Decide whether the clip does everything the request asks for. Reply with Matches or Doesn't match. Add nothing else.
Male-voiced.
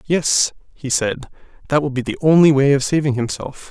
Matches